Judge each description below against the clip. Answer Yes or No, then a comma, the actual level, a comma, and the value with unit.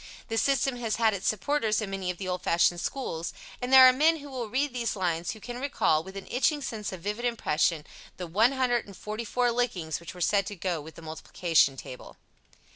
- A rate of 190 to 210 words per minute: Yes, fast, 205 wpm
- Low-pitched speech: No, high, 210 Hz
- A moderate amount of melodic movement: No, wide, 5.9 semitones